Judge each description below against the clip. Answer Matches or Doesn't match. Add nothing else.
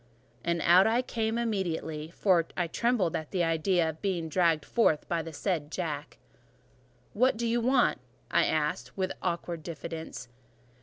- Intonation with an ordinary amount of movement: Matches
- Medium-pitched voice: Matches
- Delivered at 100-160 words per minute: Matches